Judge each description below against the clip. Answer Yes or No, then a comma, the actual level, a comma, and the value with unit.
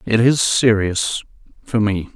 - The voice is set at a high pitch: No, low, 110 Hz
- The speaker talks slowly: Yes, slow, 110 wpm